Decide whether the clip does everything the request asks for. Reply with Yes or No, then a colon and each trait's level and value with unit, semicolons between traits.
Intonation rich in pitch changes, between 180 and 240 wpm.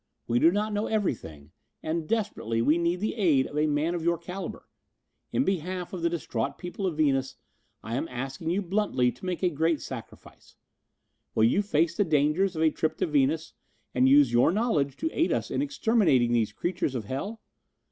Yes: wide, 5.8 semitones; average, 195 wpm